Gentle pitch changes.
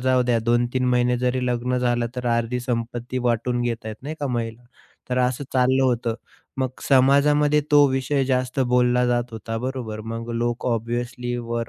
Yes: narrow, 1.4 semitones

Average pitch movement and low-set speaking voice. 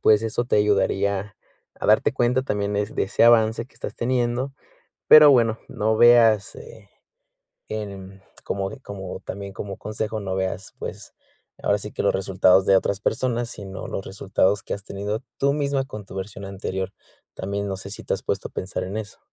Yes: average, 3.2 semitones; low, 105 Hz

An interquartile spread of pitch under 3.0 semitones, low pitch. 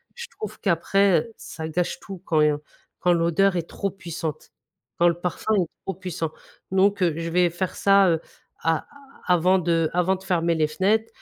No: narrow, 2.5 semitones; medium, 175 Hz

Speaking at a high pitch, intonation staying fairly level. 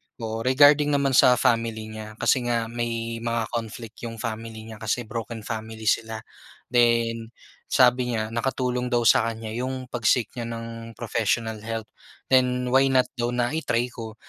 No: low, 115 Hz; narrow, 1.8 semitones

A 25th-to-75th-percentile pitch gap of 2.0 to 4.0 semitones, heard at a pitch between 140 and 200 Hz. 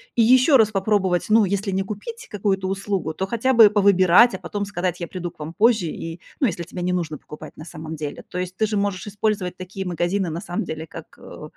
Yes: average, 3.2 semitones; high, 190 Hz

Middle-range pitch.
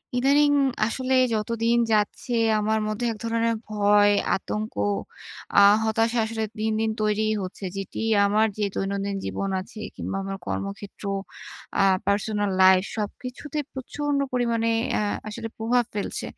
No: high, 220 Hz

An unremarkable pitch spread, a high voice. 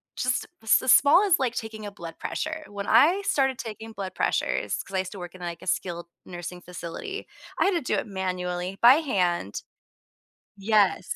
No: wide, 6.3 semitones; high, 200 Hz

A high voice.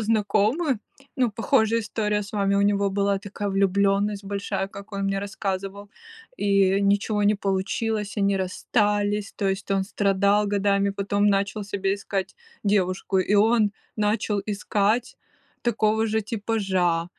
Yes: high, 200 Hz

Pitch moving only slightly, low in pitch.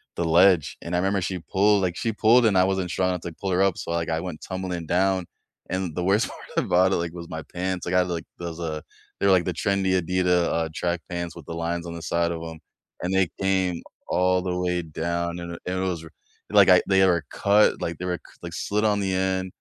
Yes: narrow, 1.8 semitones; very low, 90 Hz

